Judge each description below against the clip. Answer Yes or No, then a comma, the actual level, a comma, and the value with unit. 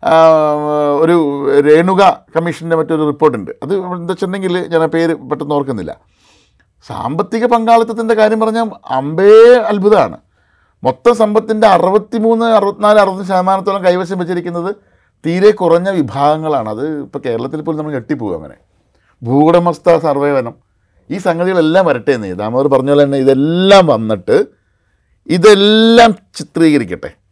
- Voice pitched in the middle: Yes, medium, 170 Hz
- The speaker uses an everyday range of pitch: No, wide, 5.8 semitones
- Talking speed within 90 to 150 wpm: Yes, average, 110 wpm